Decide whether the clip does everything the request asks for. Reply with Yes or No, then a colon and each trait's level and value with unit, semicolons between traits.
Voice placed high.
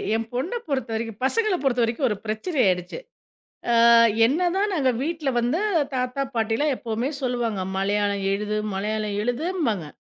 Yes: high, 240 Hz